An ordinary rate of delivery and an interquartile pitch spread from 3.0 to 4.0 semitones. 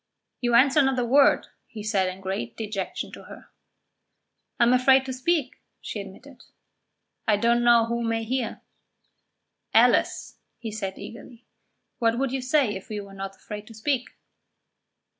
Yes: average, 160 wpm; average, 3.6 semitones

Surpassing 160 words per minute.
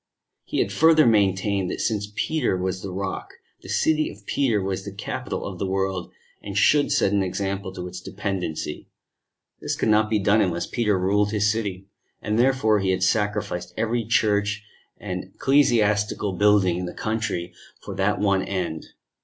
Yes: average, 170 wpm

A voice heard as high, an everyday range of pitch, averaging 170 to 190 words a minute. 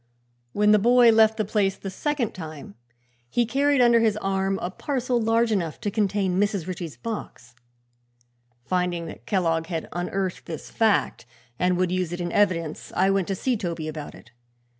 Yes: high, 195 Hz; average, 4.1 semitones; average, 175 wpm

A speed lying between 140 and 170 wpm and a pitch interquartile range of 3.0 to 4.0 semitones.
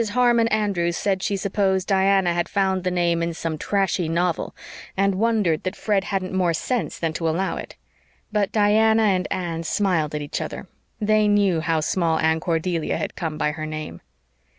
No: average, 180 wpm; average, 3.5 semitones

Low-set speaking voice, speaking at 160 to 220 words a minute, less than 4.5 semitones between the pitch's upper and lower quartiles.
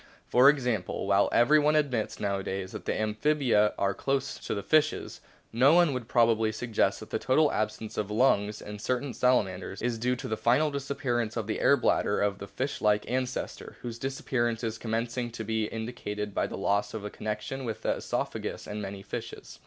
Yes: low, 115 Hz; average, 190 wpm; average, 3.5 semitones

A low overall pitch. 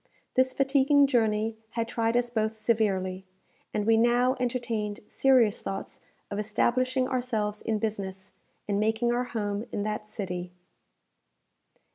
No: high, 225 Hz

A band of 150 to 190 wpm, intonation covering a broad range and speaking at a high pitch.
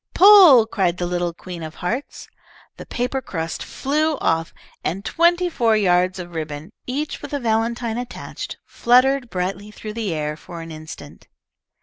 Yes: average, 155 wpm; wide, 6.5 semitones; high, 210 Hz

